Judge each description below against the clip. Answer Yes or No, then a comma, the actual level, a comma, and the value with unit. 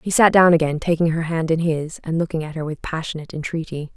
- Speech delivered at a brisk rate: Yes, fast, 240 wpm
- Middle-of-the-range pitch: Yes, medium, 160 Hz